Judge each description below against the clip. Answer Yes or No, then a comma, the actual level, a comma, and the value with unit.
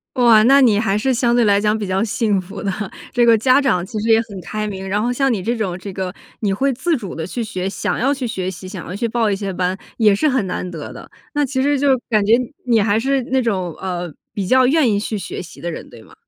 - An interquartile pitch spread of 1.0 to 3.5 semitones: No, average, 4.2 semitones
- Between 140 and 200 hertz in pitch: No, high, 215 Hz